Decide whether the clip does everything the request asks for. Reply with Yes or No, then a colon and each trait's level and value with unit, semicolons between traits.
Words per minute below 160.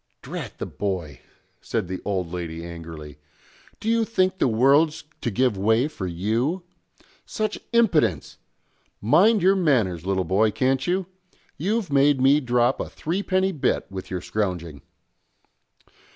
Yes: slow, 135 wpm